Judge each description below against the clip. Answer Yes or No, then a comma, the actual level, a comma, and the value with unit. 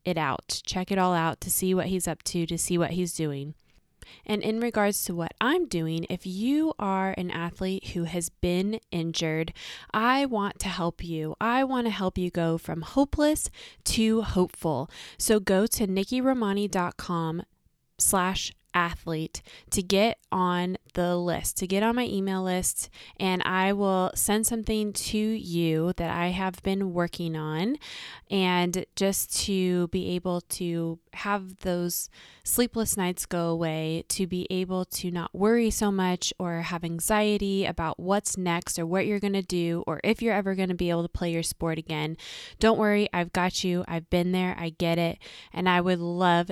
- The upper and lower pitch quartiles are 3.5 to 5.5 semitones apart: No, average, 2.8 semitones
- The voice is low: No, medium, 185 Hz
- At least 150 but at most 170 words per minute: No, average, 180 wpm